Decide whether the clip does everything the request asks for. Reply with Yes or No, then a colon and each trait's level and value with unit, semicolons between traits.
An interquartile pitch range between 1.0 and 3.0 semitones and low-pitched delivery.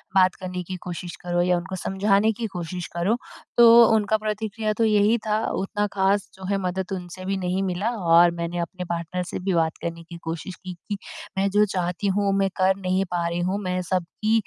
No: narrow, 2.6 semitones; high, 190 Hz